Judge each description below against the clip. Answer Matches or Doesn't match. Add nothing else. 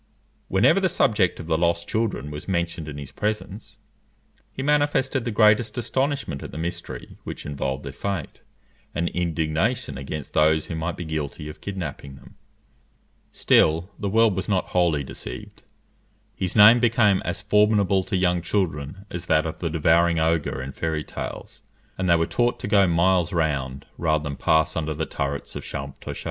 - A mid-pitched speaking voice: Doesn't match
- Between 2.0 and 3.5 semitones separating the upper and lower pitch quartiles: Doesn't match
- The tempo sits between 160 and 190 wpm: Matches